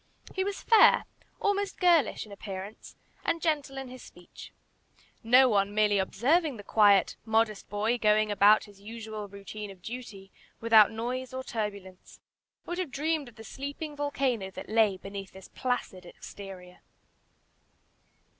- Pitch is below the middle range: No, high, 220 Hz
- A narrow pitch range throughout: No, average, 4.9 semitones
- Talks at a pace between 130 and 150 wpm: Yes, average, 145 wpm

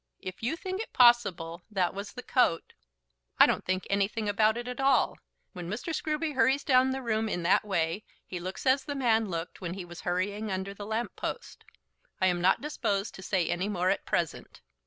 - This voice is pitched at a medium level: No, high, 205 Hz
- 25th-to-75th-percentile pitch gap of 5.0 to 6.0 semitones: Yes, wide, 5.4 semitones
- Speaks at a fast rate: Yes, fast, 210 wpm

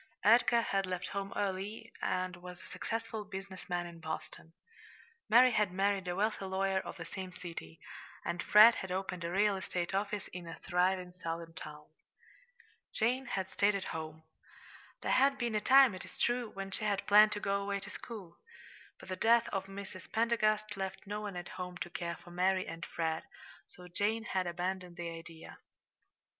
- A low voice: No, high, 190 Hz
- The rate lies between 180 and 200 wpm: Yes, average, 185 wpm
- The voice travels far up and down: No, average, 2.8 semitones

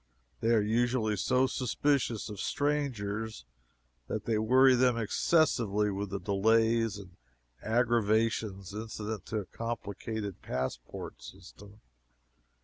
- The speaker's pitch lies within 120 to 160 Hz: No, low, 110 Hz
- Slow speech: Yes, slow, 110 wpm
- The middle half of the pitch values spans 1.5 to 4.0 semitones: Yes, narrow, 2.6 semitones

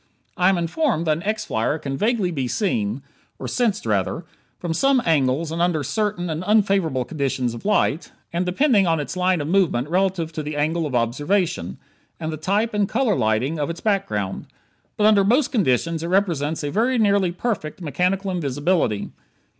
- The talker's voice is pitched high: No, medium, 170 Hz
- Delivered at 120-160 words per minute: No, average, 180 wpm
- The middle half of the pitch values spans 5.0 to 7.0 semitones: Yes, average, 5.3 semitones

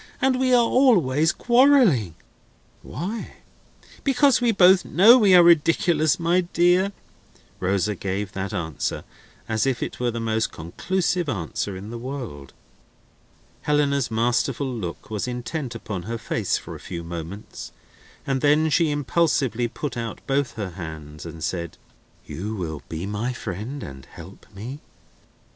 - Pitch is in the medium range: No, low, 125 Hz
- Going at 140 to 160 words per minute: Yes, average, 145 wpm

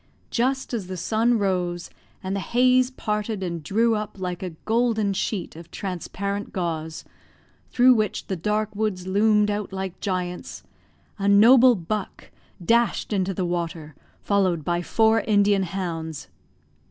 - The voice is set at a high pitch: Yes, high, 200 Hz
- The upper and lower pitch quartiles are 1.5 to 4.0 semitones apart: Yes, average, 3.5 semitones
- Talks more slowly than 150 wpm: Yes, average, 140 wpm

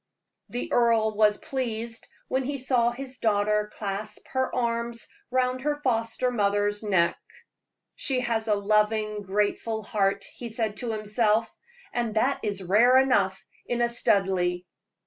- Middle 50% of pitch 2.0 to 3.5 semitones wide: Yes, average, 2.8 semitones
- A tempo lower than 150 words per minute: Yes, average, 140 wpm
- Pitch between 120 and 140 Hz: No, high, 220 Hz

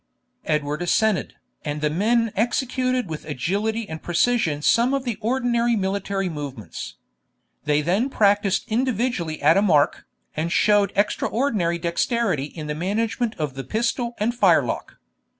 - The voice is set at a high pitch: Yes, high, 200 Hz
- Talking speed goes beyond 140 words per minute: No, slow, 135 wpm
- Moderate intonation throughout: No, wide, 6.7 semitones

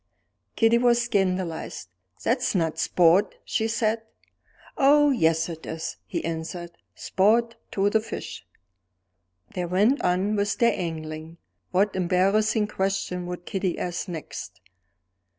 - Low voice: No, high, 190 Hz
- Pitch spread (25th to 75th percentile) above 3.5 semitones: Yes, average, 4.4 semitones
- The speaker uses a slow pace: Yes, slow, 120 wpm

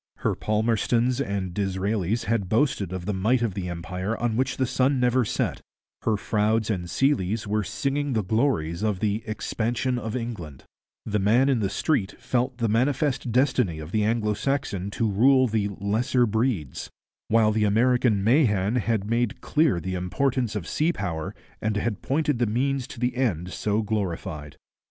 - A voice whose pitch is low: Yes, low, 110 Hz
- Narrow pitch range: No, average, 4.0 semitones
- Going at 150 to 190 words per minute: Yes, average, 170 wpm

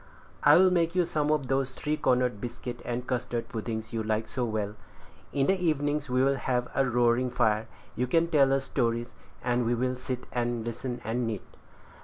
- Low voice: Yes, low, 125 Hz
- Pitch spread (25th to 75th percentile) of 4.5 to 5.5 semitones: No, narrow, 2.6 semitones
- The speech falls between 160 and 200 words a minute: Yes, average, 180 wpm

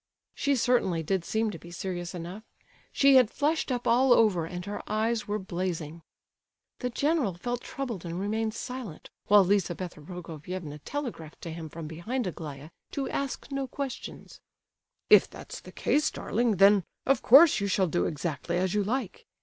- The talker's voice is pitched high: Yes, high, 200 Hz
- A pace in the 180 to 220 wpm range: No, average, 165 wpm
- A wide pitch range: Yes, wide, 6.2 semitones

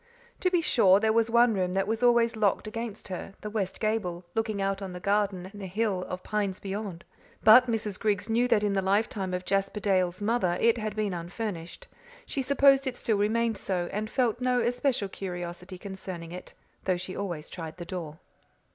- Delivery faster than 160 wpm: Yes, average, 200 wpm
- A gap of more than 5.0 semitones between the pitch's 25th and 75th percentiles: No, average, 3.5 semitones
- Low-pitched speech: No, high, 205 Hz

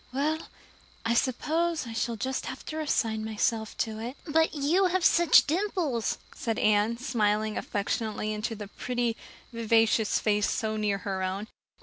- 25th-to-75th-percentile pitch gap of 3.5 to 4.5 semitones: No, average, 5.1 semitones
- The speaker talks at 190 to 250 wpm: No, average, 150 wpm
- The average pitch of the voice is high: Yes, high, 230 Hz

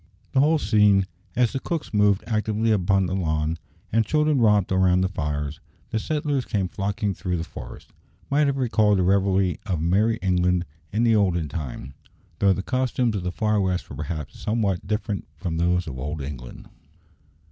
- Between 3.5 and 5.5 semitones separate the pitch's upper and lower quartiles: Yes, average, 3.9 semitones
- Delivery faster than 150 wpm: Yes, average, 180 wpm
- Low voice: Yes, low, 100 Hz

